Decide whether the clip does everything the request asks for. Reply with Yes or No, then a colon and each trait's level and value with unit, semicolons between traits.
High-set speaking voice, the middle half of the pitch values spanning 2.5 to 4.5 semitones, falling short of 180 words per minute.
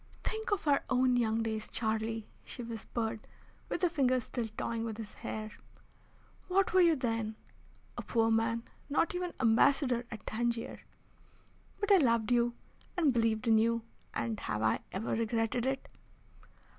Yes: high, 230 Hz; average, 2.8 semitones; average, 155 wpm